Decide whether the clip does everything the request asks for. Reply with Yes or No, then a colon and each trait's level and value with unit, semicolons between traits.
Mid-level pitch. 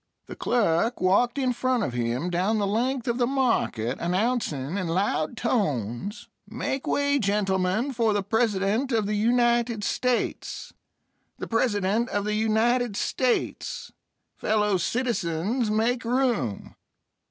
No: high, 220 Hz